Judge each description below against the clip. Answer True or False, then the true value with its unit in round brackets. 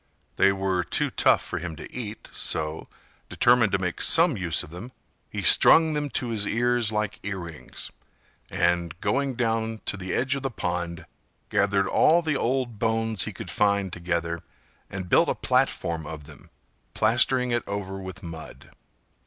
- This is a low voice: True (100 Hz)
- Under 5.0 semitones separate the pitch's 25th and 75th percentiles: False (5.3 semitones)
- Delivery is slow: False (165 wpm)